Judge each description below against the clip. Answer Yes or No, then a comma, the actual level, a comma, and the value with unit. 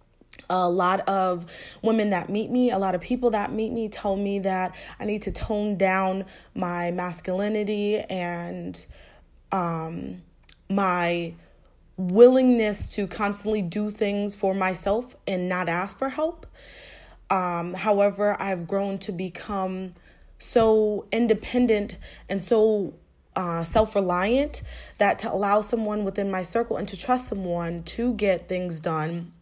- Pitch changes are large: No, average, 2.9 semitones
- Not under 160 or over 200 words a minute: No, slow, 135 wpm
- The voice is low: No, high, 195 Hz